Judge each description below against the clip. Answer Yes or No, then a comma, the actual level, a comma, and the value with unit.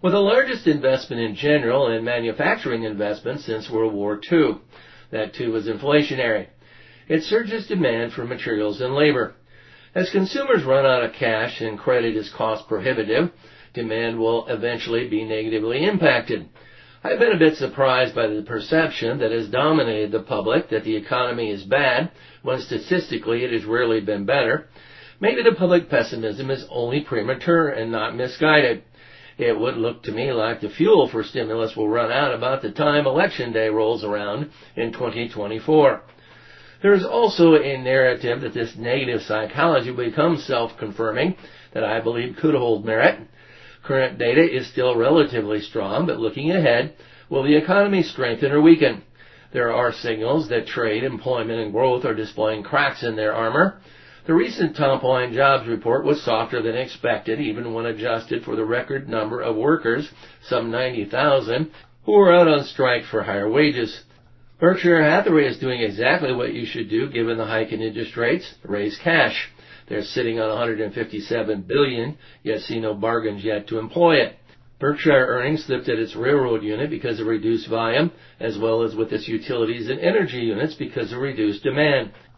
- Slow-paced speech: No, average, 170 wpm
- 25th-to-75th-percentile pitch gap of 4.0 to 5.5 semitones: Yes, average, 4.8 semitones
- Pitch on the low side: Yes, low, 120 Hz